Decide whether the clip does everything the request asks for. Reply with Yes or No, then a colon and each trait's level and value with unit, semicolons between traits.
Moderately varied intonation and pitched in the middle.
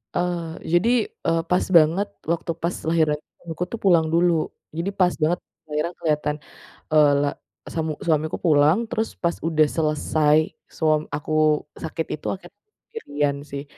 No: narrow, 2.3 semitones; medium, 160 Hz